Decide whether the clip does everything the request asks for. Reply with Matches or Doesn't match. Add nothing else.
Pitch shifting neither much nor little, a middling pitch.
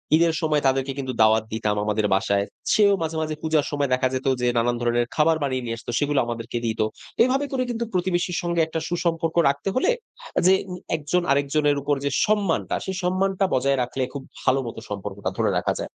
Doesn't match